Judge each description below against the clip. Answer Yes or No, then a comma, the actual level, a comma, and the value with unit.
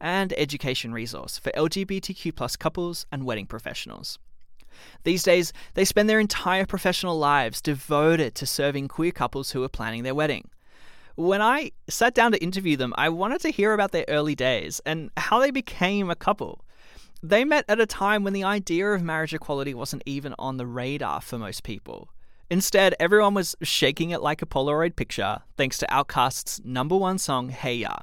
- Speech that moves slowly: No, average, 180 wpm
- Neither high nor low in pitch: Yes, medium, 160 Hz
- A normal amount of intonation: No, wide, 5.9 semitones